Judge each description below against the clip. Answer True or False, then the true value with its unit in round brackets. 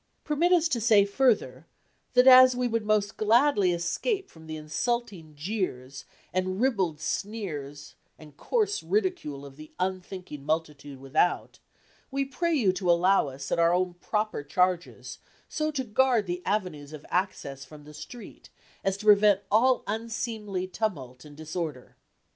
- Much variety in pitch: True (7.0 semitones)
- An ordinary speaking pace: True (150 wpm)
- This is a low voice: False (185 Hz)